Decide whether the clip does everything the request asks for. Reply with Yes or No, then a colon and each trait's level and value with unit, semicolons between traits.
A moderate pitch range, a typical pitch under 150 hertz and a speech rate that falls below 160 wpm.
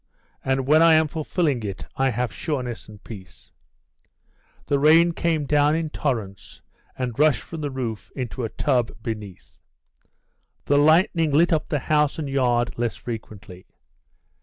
Yes: average, 4.7 semitones; low, 135 Hz; average, 150 wpm